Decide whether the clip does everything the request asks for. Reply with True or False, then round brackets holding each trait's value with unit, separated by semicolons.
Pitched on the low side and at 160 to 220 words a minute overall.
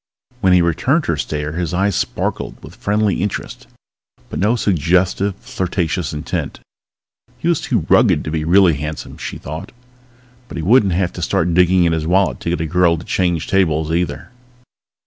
True (90 Hz; 175 wpm)